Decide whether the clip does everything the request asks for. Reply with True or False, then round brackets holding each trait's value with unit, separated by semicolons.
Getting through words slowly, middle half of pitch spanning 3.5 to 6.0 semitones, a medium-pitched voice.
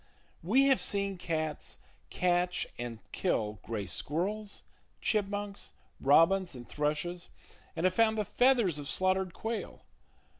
True (120 wpm; 5.2 semitones; 180 Hz)